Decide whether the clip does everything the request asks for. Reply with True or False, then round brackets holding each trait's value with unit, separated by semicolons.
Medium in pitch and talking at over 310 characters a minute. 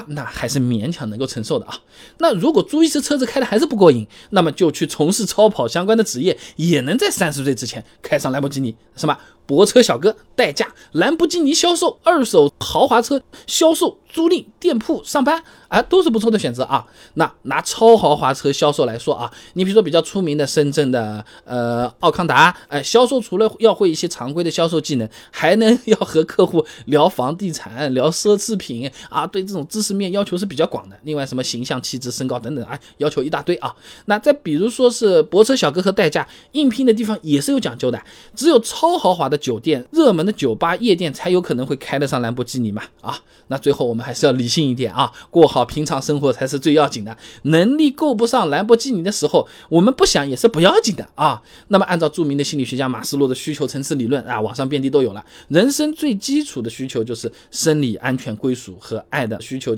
True (160 Hz; 330 characters per minute)